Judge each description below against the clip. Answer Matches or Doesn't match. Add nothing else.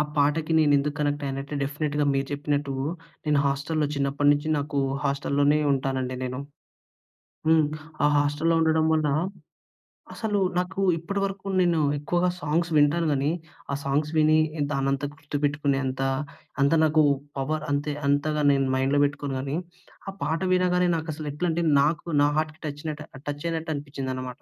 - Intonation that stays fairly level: Matches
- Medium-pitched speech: Matches